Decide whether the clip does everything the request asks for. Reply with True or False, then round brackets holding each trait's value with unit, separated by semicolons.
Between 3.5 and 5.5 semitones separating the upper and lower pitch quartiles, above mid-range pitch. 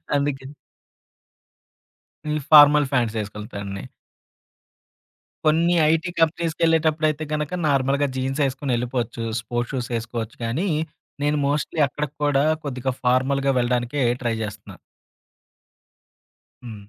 False (3.8 semitones; 135 Hz)